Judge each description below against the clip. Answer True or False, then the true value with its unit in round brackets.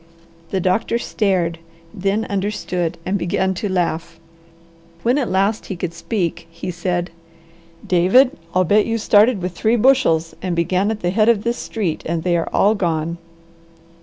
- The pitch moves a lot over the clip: False (3.6 semitones)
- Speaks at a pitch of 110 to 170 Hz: False (185 Hz)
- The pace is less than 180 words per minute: True (165 wpm)